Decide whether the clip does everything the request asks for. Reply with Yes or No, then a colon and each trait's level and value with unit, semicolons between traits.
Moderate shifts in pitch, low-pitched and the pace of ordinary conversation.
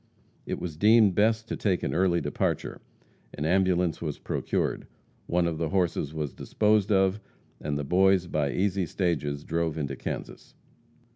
Yes: average, 3.8 semitones; very low, 90 Hz; average, 155 wpm